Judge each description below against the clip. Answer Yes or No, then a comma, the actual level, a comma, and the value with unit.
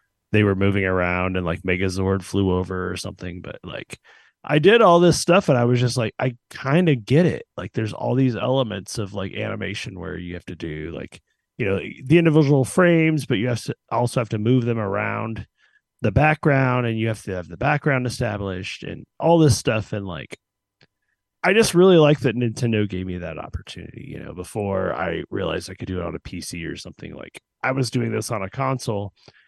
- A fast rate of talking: Yes, fast, 215 wpm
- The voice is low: Yes, low, 110 Hz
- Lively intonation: Yes, wide, 5.9 semitones